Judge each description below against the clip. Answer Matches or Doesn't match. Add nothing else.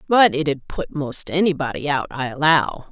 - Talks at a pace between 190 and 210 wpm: Doesn't match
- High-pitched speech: Doesn't match